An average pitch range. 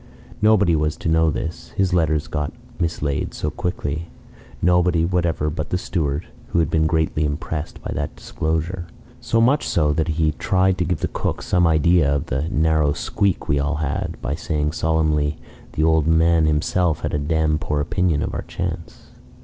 No: narrow, 2.3 semitones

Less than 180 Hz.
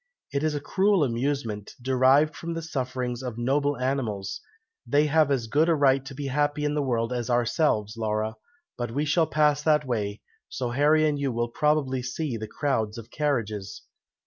Yes: low, 135 Hz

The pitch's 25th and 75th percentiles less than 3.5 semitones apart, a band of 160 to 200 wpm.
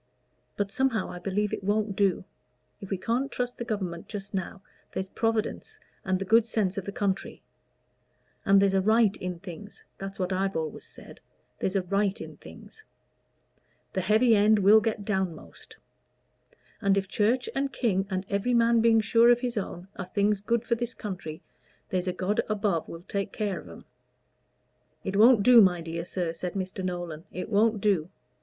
Yes: average, 2.9 semitones; average, 180 wpm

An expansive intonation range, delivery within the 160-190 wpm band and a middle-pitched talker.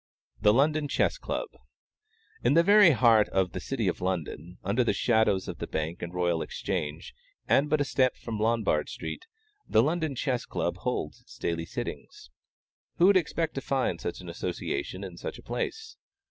No: wide, 8.4 semitones; average, 180 wpm; low, 110 Hz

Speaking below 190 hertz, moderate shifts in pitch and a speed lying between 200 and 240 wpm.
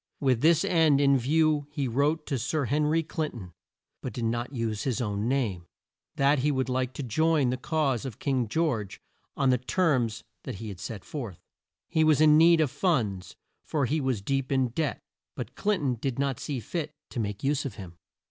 Yes: low, 135 Hz; average, 4.4 semitones; fast, 205 wpm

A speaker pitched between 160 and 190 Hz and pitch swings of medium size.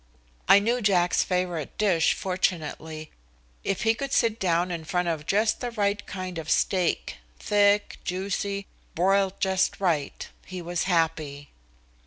Yes: medium, 185 Hz; average, 3.3 semitones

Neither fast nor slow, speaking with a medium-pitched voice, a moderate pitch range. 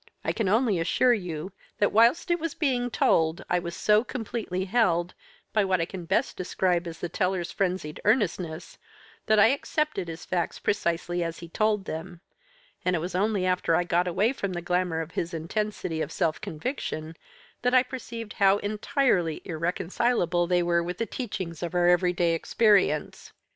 Yes: average, 175 wpm; medium, 180 Hz; average, 4.1 semitones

